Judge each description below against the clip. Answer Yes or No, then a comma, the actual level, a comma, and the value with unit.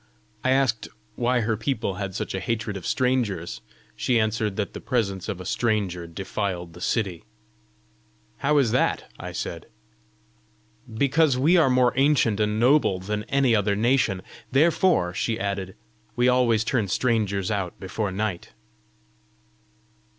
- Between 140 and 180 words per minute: Yes, average, 145 wpm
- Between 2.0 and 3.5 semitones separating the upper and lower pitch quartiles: No, average, 4.5 semitones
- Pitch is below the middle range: Yes, low, 110 Hz